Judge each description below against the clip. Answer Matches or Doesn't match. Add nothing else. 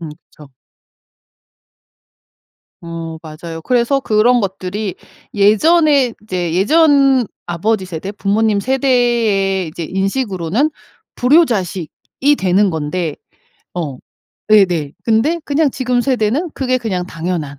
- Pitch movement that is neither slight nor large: Doesn't match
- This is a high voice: Matches